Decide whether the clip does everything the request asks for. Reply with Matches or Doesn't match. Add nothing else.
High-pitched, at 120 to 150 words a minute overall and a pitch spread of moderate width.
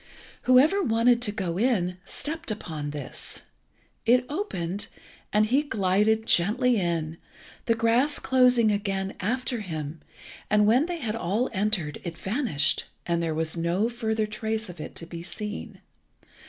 Doesn't match